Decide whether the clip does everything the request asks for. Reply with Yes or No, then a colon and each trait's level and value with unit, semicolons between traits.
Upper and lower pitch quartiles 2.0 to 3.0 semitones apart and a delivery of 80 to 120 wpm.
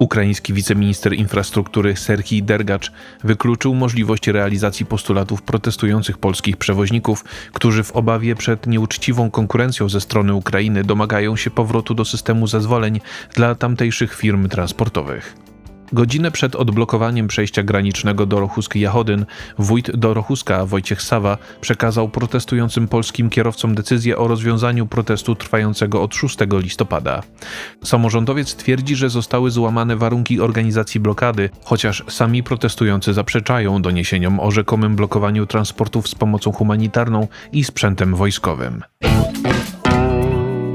Yes: narrow, 2.4 semitones; average, 115 wpm